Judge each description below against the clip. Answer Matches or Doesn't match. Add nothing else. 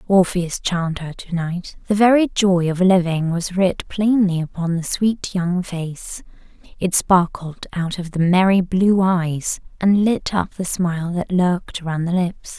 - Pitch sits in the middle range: Matches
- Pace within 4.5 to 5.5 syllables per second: Doesn't match